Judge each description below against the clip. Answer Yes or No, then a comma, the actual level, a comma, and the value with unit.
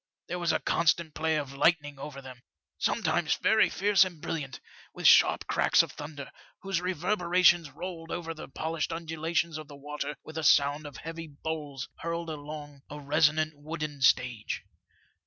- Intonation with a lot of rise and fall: No, narrow, 2.5 semitones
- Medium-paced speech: Yes, average, 160 wpm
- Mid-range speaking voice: Yes, medium, 155 Hz